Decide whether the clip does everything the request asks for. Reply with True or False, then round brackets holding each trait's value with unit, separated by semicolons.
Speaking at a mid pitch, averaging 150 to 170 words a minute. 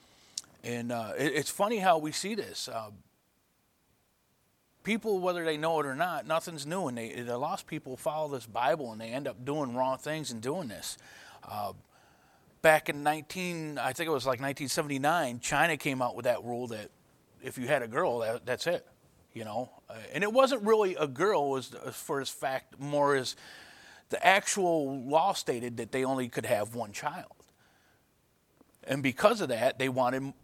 False (145 Hz; 190 wpm)